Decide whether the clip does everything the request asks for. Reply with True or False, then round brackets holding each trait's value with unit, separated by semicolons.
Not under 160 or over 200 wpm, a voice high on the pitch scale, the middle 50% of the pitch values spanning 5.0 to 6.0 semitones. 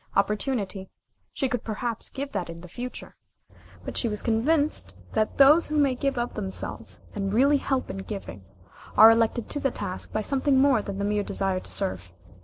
True (195 wpm; 225 Hz; 5.3 semitones)